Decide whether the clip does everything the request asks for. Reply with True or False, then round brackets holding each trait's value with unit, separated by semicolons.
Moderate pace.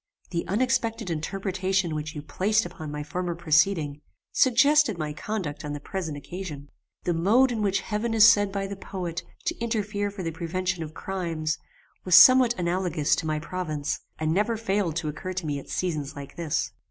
True (185 wpm)